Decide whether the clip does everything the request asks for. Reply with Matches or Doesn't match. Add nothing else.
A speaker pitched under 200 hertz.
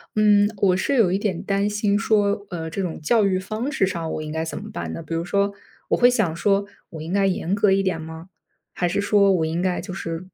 Matches